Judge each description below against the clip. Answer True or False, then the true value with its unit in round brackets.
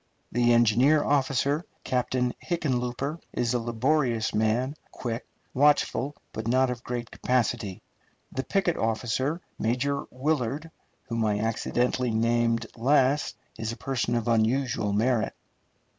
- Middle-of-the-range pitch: False (125 Hz)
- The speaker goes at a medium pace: False (120 wpm)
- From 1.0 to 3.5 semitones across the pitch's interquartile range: True (2.9 semitones)